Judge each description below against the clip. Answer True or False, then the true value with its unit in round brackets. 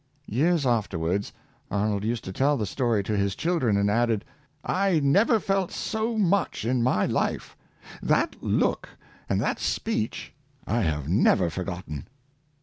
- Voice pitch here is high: False (115 Hz)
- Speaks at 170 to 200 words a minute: False (150 wpm)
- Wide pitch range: True (7.6 semitones)